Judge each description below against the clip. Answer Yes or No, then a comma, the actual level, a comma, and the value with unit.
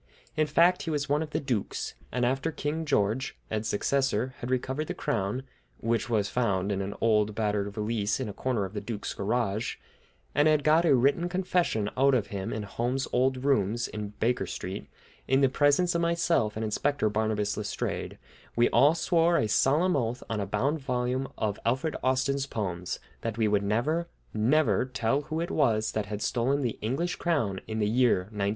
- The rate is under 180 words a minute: No, average, 190 wpm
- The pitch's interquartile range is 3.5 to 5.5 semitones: Yes, average, 5.2 semitones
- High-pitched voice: No, low, 125 Hz